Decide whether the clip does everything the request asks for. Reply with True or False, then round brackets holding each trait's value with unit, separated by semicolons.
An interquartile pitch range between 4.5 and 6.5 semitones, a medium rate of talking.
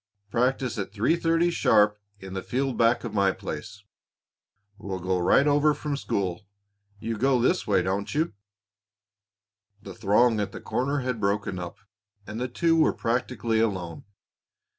True (5.1 semitones; 155 wpm)